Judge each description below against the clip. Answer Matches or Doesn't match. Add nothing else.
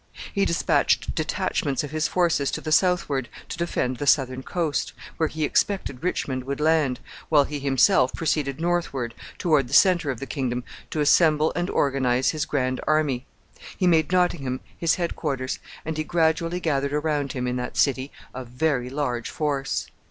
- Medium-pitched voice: Matches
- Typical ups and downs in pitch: Matches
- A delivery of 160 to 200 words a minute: Matches